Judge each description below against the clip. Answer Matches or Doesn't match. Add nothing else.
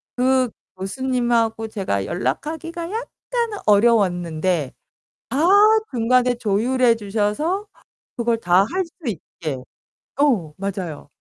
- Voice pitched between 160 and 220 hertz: Doesn't match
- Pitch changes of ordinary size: Doesn't match